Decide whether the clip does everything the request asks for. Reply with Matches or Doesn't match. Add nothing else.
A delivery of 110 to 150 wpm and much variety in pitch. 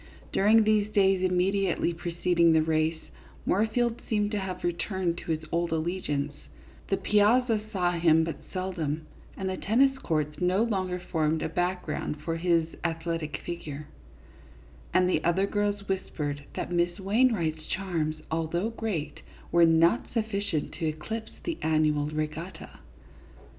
Doesn't match